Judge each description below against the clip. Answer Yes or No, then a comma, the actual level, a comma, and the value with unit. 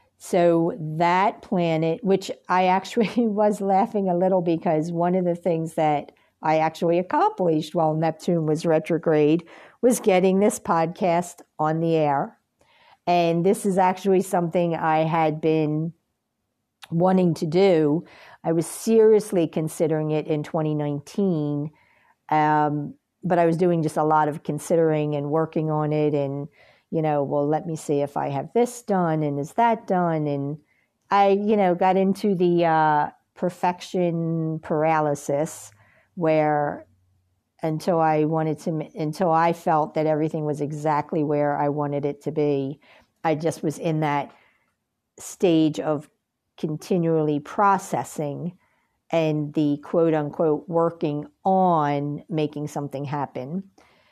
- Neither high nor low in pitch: Yes, medium, 160 Hz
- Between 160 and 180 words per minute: No, slow, 135 wpm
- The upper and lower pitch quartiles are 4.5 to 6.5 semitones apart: No, average, 2.9 semitones